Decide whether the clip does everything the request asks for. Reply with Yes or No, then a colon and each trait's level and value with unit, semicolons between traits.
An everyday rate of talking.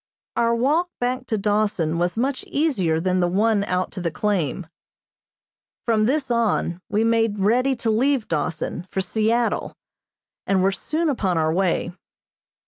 Yes: average, 150 wpm